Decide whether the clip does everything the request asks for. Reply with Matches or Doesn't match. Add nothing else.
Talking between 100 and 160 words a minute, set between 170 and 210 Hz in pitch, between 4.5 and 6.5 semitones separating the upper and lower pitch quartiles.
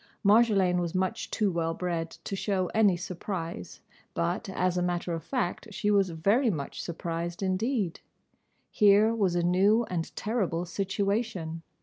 Doesn't match